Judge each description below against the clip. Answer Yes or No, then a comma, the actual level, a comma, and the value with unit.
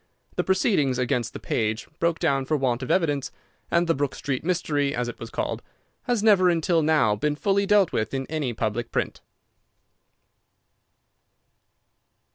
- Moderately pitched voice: Yes, medium, 145 Hz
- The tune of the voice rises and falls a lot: Yes, wide, 5.7 semitones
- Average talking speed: Yes, average, 155 wpm